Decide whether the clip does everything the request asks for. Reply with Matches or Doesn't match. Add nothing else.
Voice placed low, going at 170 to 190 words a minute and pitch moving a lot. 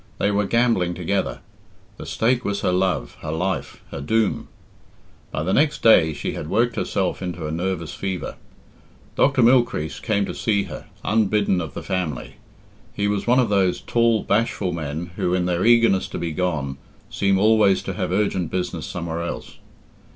Doesn't match